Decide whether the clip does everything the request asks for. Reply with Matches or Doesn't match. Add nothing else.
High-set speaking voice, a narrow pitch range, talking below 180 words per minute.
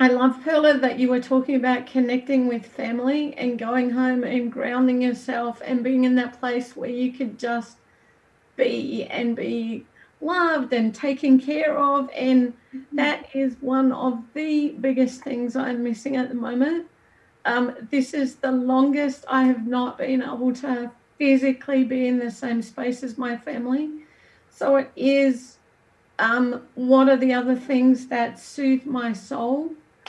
Matches